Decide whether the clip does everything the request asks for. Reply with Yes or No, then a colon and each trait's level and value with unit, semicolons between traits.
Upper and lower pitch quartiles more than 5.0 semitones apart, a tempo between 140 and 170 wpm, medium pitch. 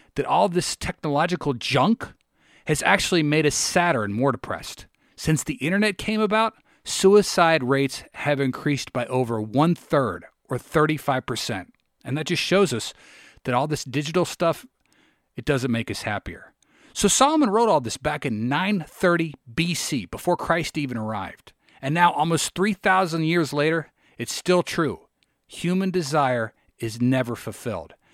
Yes: wide, 5.6 semitones; average, 150 wpm; medium, 150 Hz